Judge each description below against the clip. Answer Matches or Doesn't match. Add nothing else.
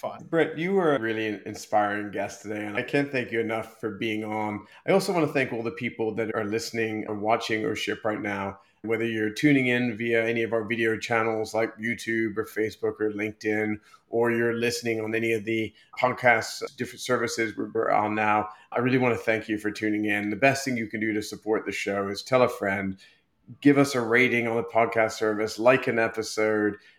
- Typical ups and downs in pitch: Doesn't match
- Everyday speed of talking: Doesn't match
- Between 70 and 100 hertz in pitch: Doesn't match